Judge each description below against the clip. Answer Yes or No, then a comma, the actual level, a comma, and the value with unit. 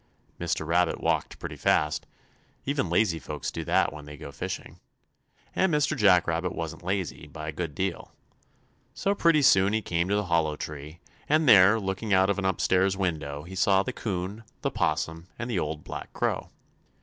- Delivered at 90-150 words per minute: No, average, 185 wpm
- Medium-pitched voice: No, very low, 90 Hz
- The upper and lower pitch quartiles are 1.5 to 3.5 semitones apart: No, average, 4.0 semitones